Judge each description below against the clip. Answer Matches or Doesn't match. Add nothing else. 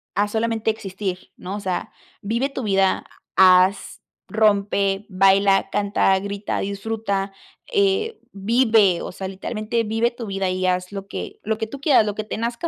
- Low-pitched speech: Doesn't match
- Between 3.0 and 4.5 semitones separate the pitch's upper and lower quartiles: Doesn't match